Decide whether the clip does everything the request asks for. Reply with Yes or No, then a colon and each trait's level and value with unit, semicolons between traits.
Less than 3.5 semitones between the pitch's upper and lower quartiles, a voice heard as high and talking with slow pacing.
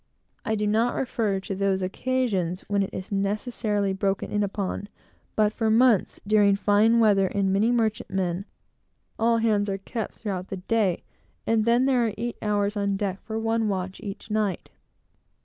No: narrow, 2.4 semitones; high, 205 Hz; average, 165 wpm